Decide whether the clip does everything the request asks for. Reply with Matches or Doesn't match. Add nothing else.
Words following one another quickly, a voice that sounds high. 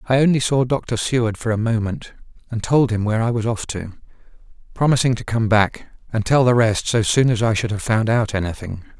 Doesn't match